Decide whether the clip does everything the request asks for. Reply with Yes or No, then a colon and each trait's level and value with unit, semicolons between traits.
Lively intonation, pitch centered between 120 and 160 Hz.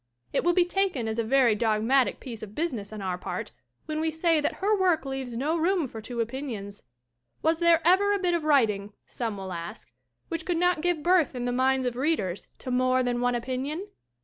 No: wide, 6.4 semitones; very high, 265 Hz